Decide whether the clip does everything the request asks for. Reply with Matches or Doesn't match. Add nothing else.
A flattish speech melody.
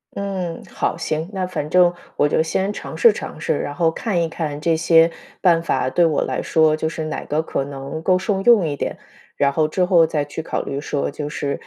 Doesn't match